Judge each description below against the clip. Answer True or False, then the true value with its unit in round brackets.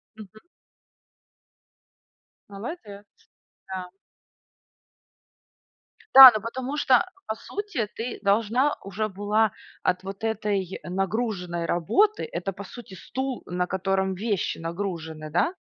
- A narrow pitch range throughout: False (3.7 semitones)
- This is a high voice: True (205 Hz)